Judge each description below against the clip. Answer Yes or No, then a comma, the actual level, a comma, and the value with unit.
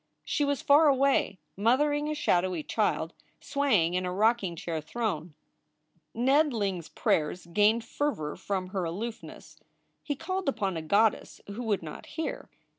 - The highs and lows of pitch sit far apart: Yes, wide, 7.7 semitones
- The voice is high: Yes, high, 210 Hz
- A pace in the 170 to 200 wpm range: No, average, 150 wpm